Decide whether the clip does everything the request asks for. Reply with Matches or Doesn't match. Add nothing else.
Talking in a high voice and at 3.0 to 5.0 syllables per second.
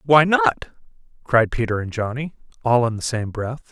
Doesn't match